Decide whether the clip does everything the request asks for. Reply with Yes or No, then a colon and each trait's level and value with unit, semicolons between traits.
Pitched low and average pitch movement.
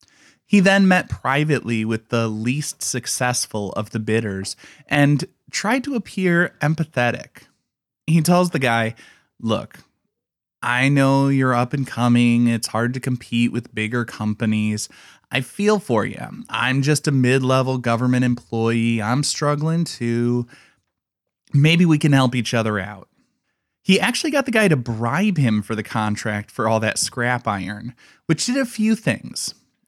Yes: low, 125 Hz; average, 4.8 semitones